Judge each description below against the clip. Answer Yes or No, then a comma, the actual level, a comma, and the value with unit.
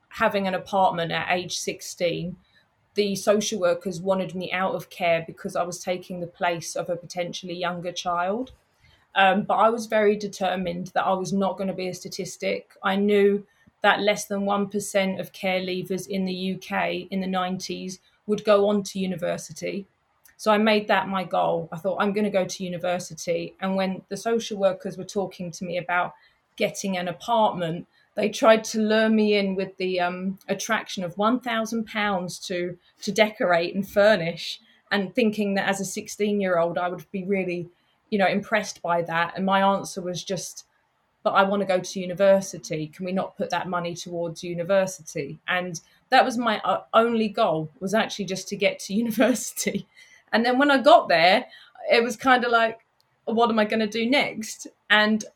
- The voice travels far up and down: No, average, 2.7 semitones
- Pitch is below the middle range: No, high, 190 Hz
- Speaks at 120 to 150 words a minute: No, average, 185 wpm